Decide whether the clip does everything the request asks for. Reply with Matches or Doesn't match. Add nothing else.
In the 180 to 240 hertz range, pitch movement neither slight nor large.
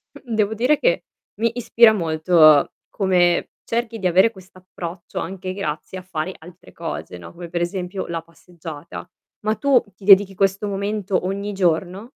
Matches